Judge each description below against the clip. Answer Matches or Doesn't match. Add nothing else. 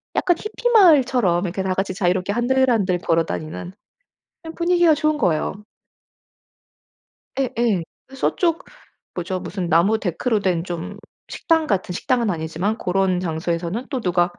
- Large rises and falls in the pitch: Matches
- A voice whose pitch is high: Matches